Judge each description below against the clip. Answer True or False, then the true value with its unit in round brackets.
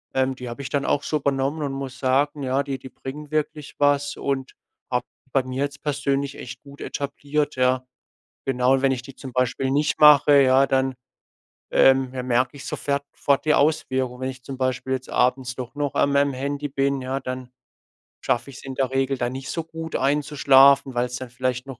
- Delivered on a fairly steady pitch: True (1.6 semitones)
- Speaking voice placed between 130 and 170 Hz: True (135 Hz)